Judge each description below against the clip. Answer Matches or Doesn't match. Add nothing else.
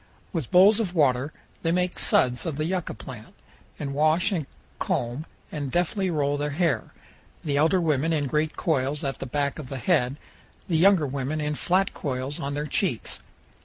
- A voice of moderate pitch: Matches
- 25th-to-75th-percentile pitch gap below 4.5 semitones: Matches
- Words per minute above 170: Matches